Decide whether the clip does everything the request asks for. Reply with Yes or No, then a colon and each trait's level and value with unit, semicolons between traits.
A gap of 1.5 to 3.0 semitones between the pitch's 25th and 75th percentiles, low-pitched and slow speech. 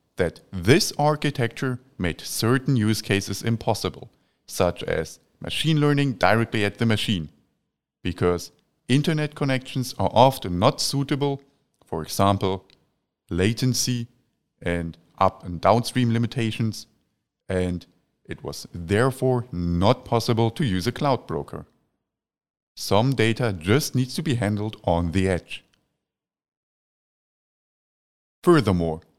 No: wide, 5.5 semitones; low, 115 Hz; slow, 110 wpm